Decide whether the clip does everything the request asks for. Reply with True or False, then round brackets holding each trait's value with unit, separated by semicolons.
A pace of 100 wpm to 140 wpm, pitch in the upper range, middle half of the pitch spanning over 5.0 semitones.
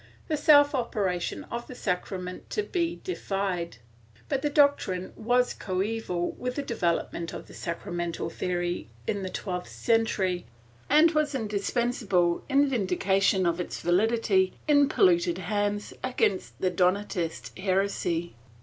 True (135 wpm; 195 Hz; 5.6 semitones)